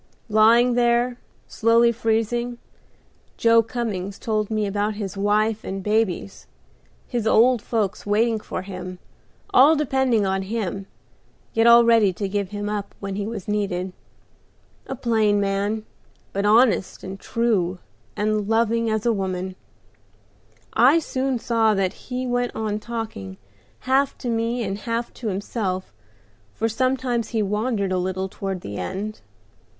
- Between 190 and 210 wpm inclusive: No, average, 145 wpm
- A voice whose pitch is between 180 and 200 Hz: No, high, 215 Hz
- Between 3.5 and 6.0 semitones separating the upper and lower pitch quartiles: No, average, 3.0 semitones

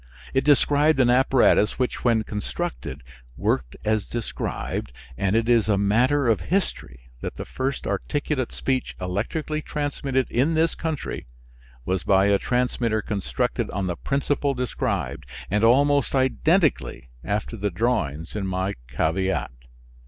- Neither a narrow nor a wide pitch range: No, wide, 6.0 semitones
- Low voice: Yes, low, 115 Hz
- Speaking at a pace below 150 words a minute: Yes, slow, 135 wpm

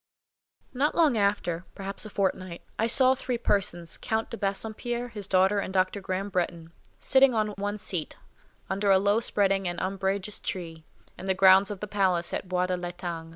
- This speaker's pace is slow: No, average, 175 wpm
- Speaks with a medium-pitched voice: No, high, 195 Hz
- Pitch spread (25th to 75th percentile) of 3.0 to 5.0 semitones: No, narrow, 2.4 semitones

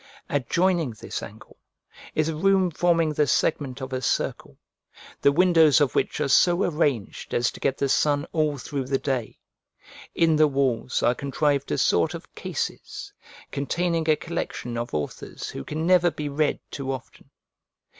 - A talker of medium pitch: Yes, medium, 145 Hz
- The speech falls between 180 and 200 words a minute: No, average, 165 wpm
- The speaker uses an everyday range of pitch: Yes, average, 3.7 semitones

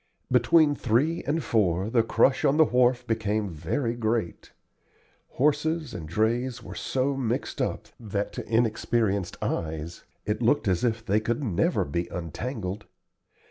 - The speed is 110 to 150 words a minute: Yes, average, 140 wpm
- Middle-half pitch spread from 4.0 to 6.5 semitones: Yes, average, 4.3 semitones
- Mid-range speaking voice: No, low, 115 Hz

